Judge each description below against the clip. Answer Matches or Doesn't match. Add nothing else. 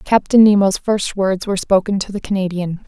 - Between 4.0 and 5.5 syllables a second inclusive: Matches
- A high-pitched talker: Matches